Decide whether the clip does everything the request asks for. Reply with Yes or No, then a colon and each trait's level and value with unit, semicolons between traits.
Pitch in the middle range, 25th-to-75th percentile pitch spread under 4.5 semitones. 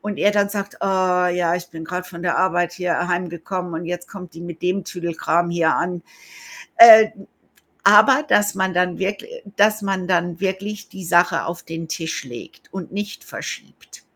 Yes: medium, 180 Hz; narrow, 2.4 semitones